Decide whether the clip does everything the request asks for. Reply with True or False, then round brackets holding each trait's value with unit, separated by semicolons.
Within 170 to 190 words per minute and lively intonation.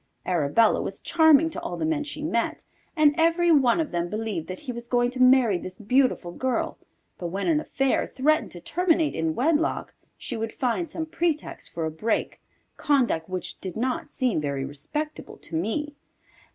True (180 wpm; 8.7 semitones)